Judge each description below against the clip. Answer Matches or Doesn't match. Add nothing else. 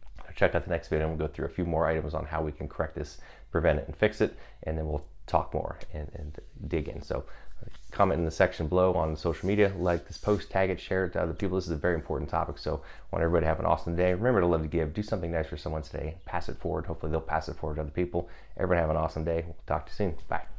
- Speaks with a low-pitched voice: Matches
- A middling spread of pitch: Doesn't match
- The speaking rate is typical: Doesn't match